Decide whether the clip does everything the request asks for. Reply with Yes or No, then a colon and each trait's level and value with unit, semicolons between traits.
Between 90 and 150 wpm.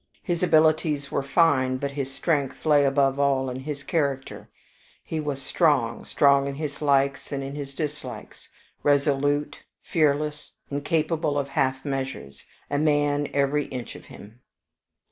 Yes: average, 145 wpm